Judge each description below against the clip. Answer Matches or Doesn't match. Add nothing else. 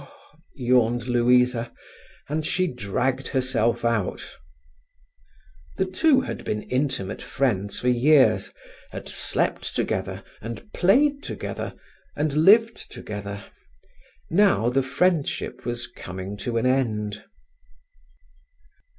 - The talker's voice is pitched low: Matches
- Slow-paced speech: Matches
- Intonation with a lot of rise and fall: Doesn't match